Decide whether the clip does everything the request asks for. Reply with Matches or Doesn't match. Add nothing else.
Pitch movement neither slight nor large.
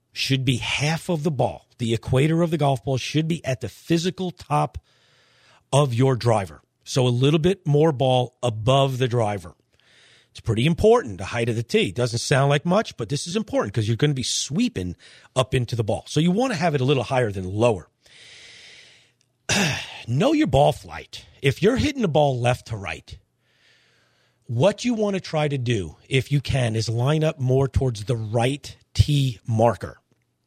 Matches